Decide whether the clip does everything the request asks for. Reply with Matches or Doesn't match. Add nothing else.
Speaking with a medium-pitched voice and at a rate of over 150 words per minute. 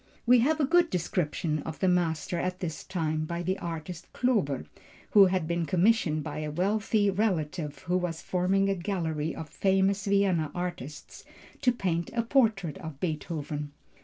Matches